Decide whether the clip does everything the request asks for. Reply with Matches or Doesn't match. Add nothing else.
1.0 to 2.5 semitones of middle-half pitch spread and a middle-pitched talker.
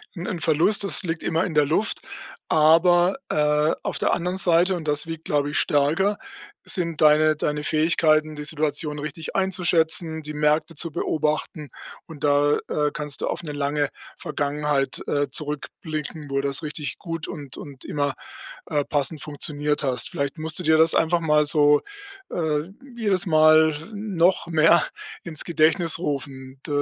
Matches